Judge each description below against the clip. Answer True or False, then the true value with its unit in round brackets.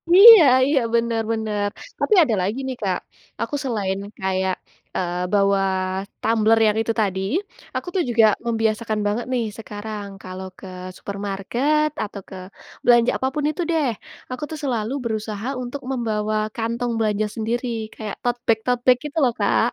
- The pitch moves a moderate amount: True (3.2 semitones)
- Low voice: False (225 Hz)